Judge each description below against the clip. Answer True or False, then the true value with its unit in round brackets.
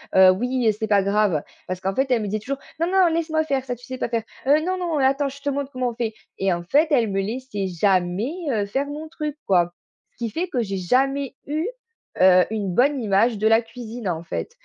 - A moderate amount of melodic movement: False (6.0 semitones)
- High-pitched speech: True (235 Hz)